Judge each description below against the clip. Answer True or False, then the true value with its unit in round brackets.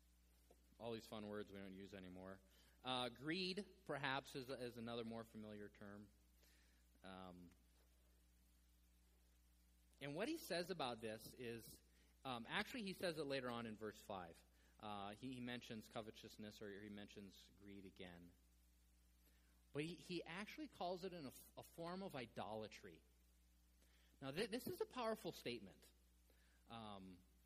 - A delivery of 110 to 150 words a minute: True (140 wpm)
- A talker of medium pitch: False (100 Hz)